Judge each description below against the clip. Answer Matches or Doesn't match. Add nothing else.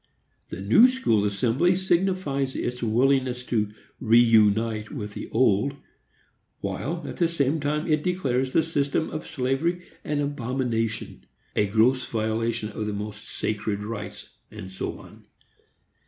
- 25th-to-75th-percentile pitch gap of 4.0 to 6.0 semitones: Matches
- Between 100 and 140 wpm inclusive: Matches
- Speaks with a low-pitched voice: Matches